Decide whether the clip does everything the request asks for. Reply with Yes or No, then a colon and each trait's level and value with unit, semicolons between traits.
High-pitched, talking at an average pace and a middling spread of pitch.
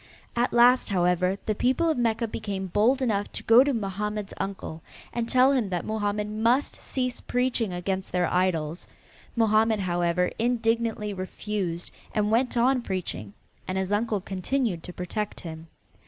Yes: high, 210 Hz; average, 155 wpm; average, 4.2 semitones